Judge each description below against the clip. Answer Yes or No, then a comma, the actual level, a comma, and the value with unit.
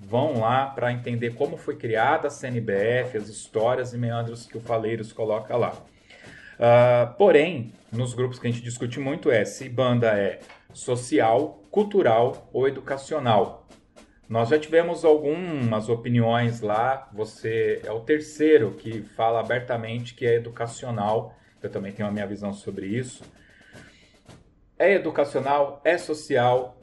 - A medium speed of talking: Yes, average, 140 wpm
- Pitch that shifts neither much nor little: Yes, average, 3.4 semitones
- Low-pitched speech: Yes, low, 120 Hz